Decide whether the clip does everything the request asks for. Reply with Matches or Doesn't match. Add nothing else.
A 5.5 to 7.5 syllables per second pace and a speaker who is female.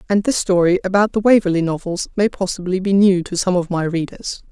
Matches